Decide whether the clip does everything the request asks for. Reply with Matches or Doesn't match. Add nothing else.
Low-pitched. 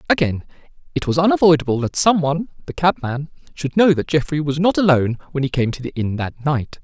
Doesn't match